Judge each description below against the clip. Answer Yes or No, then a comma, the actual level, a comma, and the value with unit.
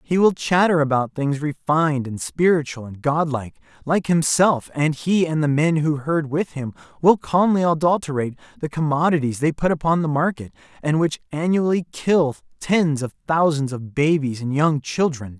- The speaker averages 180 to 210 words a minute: No, average, 170 wpm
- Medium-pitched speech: Yes, medium, 150 Hz